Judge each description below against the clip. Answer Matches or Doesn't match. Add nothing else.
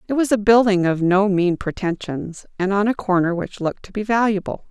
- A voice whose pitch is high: Matches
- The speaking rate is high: Matches